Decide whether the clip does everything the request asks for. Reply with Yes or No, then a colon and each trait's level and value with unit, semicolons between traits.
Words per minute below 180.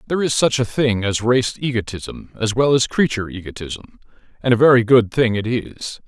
No: average, 200 wpm